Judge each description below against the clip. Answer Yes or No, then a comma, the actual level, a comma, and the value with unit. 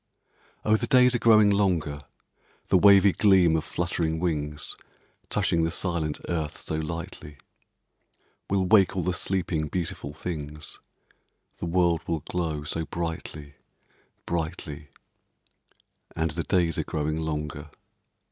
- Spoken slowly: Yes, slow, 125 wpm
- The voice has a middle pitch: No, very low, 85 Hz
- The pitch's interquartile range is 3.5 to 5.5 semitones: No, average, 3.0 semitones